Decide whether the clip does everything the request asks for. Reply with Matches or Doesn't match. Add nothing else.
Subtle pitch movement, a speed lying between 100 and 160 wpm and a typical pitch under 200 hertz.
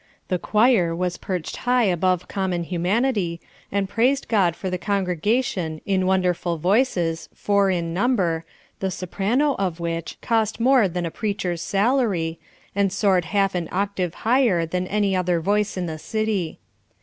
Doesn't match